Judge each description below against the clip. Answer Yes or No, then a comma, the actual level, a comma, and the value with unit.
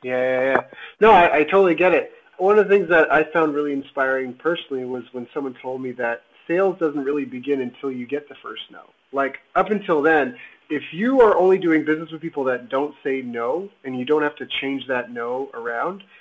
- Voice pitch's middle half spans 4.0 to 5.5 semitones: Yes, average, 4.7 semitones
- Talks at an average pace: No, fast, 220 wpm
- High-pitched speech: No, medium, 145 Hz